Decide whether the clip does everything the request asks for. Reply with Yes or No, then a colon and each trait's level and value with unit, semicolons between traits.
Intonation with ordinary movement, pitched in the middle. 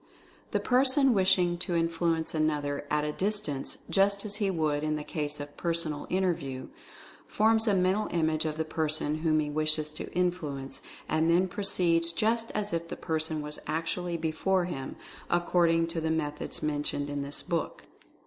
Yes: average, 3.2 semitones; medium, 165 Hz